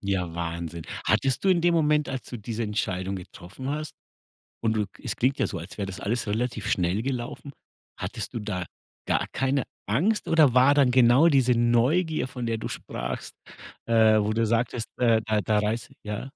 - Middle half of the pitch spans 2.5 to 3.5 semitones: No, average, 4.4 semitones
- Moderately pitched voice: No, low, 115 Hz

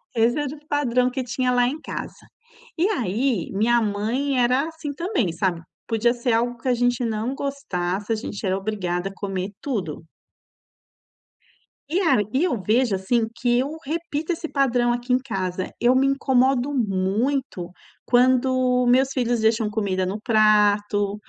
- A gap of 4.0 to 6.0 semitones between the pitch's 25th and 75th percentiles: Yes, average, 4.3 semitones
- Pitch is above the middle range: Yes, high, 240 Hz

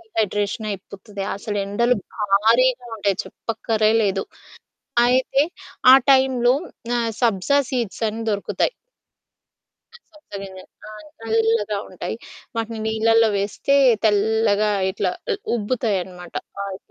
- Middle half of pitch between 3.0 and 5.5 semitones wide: No, narrow, 2.5 semitones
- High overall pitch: Yes, high, 220 Hz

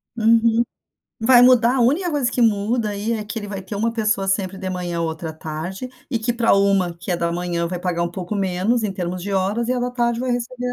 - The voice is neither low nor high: No, high, 205 Hz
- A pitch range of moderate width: Yes, average, 4.6 semitones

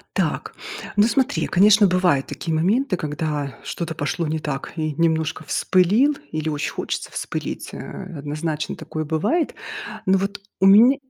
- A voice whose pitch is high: No, medium, 165 Hz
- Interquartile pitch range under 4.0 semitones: No, average, 4.5 semitones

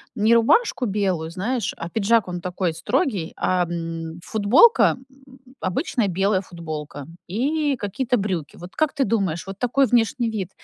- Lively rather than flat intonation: Yes, wide, 5.8 semitones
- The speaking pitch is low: No, high, 205 Hz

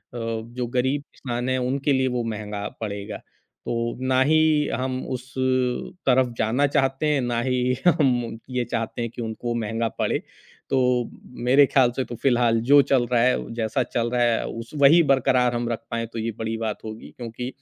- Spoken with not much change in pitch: Yes, narrow, 2.2 semitones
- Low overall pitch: Yes, low, 125 Hz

